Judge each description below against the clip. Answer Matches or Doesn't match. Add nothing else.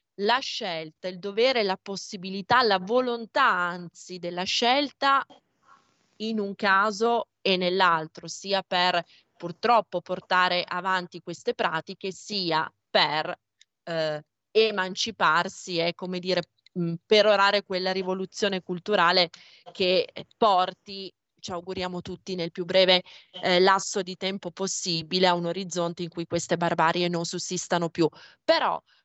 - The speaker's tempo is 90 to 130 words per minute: Matches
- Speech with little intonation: Matches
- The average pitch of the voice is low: Doesn't match